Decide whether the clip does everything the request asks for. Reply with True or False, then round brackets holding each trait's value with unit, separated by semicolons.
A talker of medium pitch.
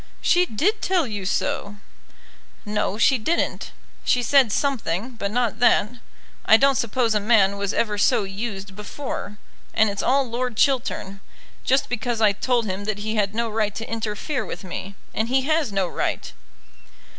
False (220 Hz)